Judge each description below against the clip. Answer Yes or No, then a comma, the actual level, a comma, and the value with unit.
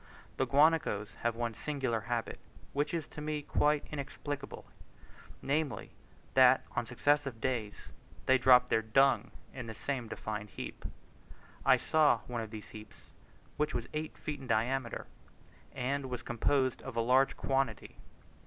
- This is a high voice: No, low, 130 Hz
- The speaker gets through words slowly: No, average, 145 wpm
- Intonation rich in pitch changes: No, average, 3.6 semitones